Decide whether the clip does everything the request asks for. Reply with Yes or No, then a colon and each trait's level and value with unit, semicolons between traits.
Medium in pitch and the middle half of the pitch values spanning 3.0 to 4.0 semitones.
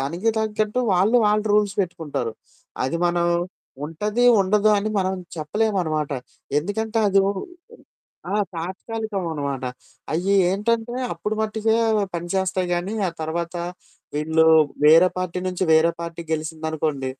No: medium, 180 Hz; average, 4.7 semitones